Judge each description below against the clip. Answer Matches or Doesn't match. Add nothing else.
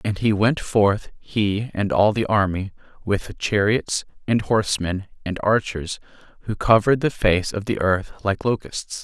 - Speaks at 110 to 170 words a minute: Matches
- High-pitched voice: Doesn't match